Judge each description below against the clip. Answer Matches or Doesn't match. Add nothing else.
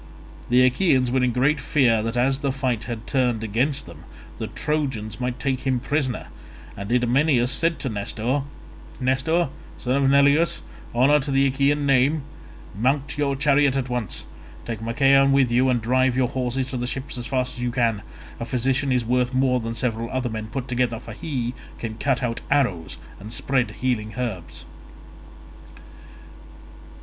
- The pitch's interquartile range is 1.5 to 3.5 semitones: Matches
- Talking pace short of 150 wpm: Doesn't match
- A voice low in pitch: Matches